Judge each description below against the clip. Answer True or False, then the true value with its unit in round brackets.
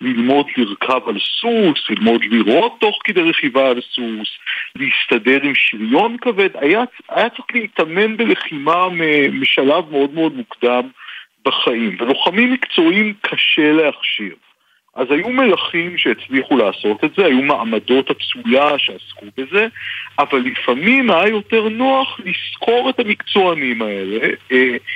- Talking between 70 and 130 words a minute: True (120 wpm)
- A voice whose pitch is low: False (185 Hz)